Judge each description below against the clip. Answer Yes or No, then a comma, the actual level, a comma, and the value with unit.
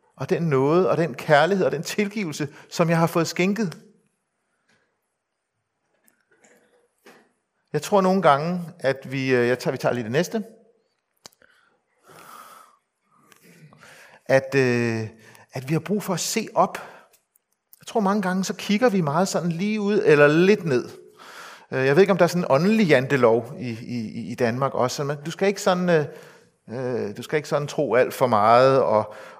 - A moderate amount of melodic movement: No, wide, 7.3 semitones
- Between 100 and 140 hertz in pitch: No, medium, 170 Hz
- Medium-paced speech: Yes, average, 160 wpm